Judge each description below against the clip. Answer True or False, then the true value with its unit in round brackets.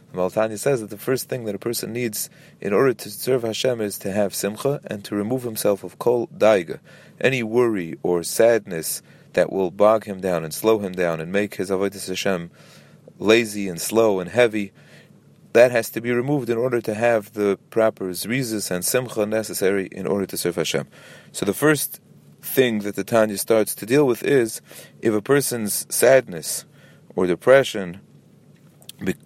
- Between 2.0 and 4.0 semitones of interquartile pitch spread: True (3.3 semitones)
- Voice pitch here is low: True (110 Hz)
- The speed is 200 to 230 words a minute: False (185 wpm)